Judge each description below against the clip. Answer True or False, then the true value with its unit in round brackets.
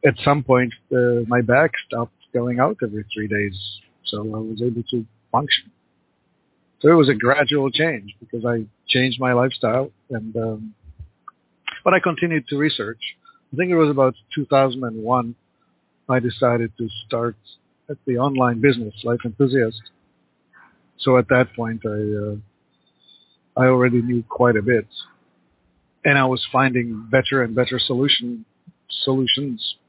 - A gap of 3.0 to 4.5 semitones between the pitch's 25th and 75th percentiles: True (3.5 semitones)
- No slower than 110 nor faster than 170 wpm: True (145 wpm)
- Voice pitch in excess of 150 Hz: False (120 Hz)